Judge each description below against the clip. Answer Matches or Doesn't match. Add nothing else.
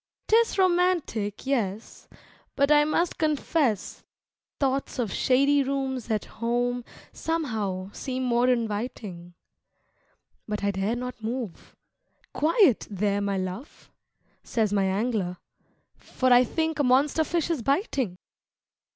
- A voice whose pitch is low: Doesn't match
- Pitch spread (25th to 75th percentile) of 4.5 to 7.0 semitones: Matches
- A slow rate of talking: Matches